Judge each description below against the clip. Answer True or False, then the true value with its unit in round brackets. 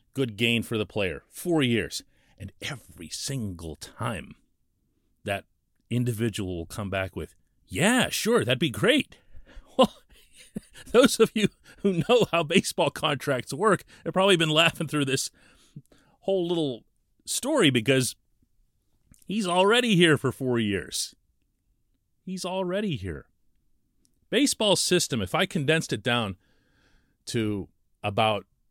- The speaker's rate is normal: False (125 wpm)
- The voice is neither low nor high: False (130 Hz)